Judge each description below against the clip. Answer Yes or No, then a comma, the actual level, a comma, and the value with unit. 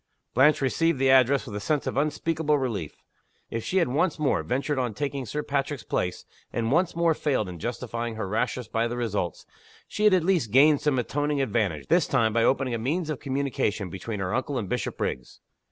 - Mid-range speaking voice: No, low, 130 Hz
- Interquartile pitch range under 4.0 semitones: No, average, 4.7 semitones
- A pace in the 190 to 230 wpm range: Yes, average, 200 wpm